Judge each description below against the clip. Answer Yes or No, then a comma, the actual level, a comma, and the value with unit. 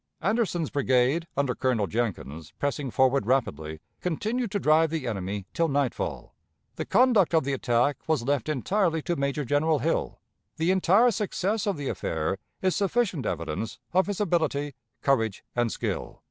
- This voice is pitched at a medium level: Yes, medium, 145 Hz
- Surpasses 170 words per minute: No, average, 155 wpm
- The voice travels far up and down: Yes, wide, 6.8 semitones